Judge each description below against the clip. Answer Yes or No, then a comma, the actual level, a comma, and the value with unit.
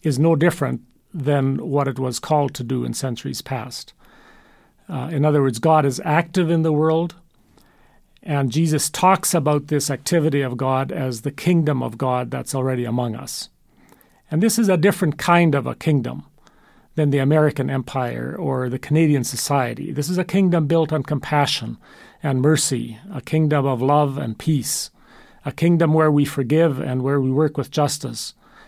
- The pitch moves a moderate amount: Yes, average, 3.3 semitones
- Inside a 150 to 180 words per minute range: Yes, average, 175 wpm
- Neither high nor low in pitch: Yes, medium, 145 Hz